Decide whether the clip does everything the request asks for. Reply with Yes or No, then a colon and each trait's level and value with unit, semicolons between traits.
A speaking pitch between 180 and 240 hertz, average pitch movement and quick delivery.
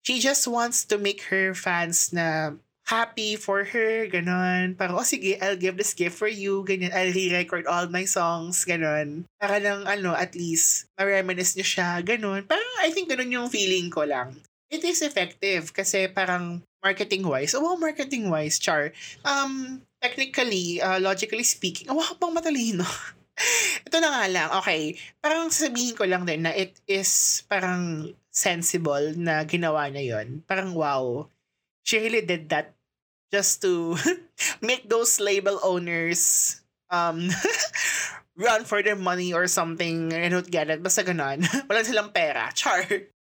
No: high, 190 Hz; average, 4.2 semitones; average, 155 wpm